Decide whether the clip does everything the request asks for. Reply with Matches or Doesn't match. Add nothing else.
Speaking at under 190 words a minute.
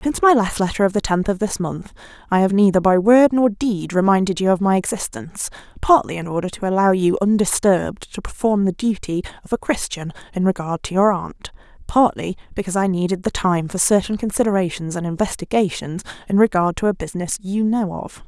Doesn't match